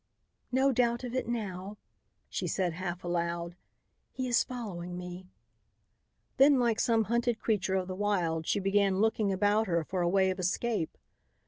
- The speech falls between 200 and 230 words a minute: No, average, 160 wpm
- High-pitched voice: Yes, high, 195 Hz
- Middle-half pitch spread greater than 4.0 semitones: Yes, average, 4.5 semitones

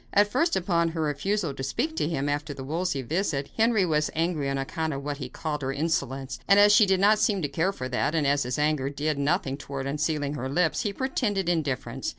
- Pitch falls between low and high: Yes, medium, 150 Hz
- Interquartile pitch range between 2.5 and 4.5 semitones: No, average, 5.2 semitones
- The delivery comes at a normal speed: No, fast, 230 wpm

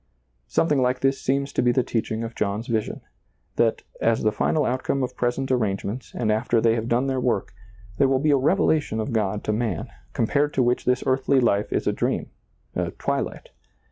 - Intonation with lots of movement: No, average, 3.3 semitones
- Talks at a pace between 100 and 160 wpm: No, fast, 205 wpm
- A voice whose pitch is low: Yes, low, 120 Hz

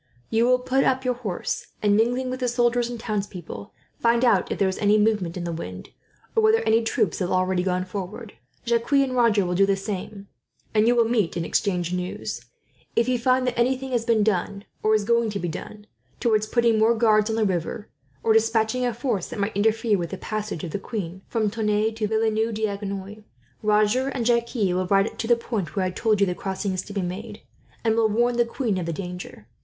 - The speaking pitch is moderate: No, high, 215 Hz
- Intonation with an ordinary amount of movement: Yes, average, 3.3 semitones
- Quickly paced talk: Yes, fast, 225 wpm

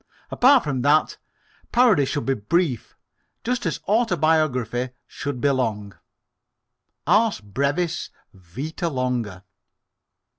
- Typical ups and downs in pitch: No, wide, 5.8 semitones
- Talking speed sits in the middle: No, slow, 100 wpm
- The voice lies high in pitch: No, medium, 140 Hz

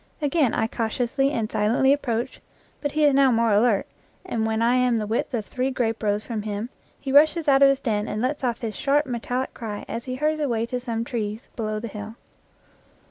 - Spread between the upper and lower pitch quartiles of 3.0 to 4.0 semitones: Yes, average, 3.6 semitones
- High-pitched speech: Yes, high, 235 Hz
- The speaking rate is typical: No, fast, 215 wpm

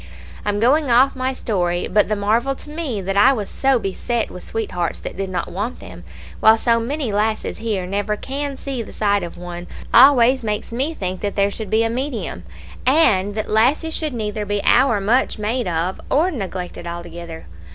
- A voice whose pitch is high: Yes, high, 215 Hz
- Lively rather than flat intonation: No, average, 4.8 semitones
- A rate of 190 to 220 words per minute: Yes, average, 195 wpm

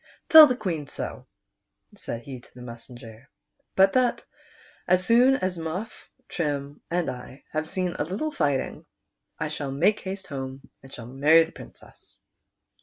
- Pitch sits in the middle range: Yes, medium, 155 Hz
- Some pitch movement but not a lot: No, wide, 6.0 semitones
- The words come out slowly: No, average, 155 wpm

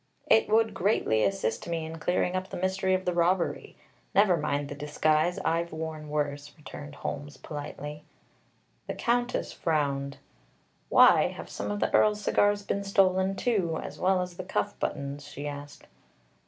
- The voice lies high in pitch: No, medium, 165 Hz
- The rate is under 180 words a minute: Yes, average, 160 wpm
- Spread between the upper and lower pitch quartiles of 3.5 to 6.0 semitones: Yes, average, 4.5 semitones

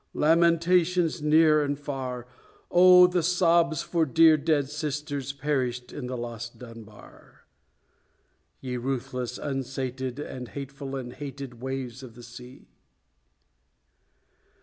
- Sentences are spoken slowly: Yes, slow, 110 wpm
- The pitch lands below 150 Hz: Yes, medium, 140 Hz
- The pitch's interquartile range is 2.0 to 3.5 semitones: No, average, 3.9 semitones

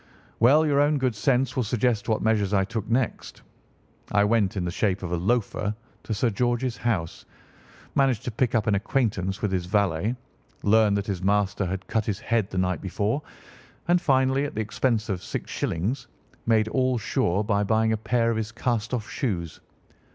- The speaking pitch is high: No, low, 110 Hz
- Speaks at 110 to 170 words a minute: No, average, 190 wpm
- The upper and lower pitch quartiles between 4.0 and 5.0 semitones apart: No, average, 3.4 semitones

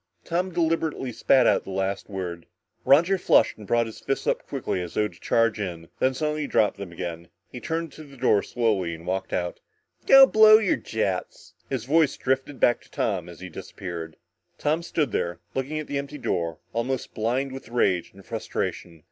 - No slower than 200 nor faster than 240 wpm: No, average, 190 wpm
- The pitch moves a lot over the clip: Yes, wide, 7.8 semitones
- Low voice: Yes, low, 115 Hz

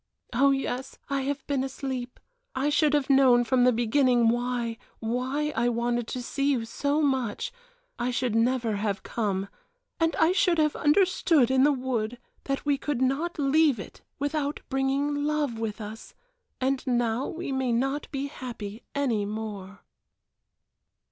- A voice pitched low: No, very high, 260 Hz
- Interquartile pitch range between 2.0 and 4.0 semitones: Yes, average, 3.3 semitones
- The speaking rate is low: No, average, 155 wpm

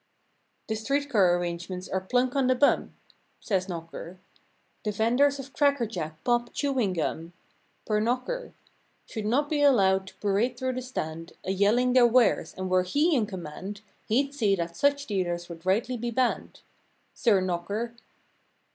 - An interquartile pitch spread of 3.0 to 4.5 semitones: No, wide, 5.5 semitones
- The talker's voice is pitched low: No, high, 215 Hz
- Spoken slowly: No, average, 165 wpm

